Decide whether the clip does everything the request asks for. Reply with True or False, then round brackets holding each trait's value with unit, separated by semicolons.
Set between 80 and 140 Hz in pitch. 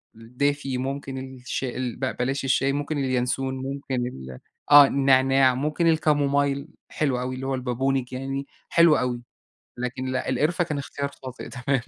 True (135 Hz)